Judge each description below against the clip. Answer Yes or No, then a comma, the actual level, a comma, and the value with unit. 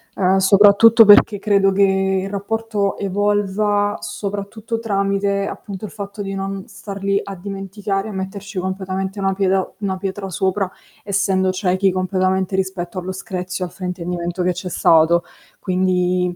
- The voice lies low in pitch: No, high, 195 Hz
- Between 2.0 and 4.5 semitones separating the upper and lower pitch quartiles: No, narrow, 1.2 semitones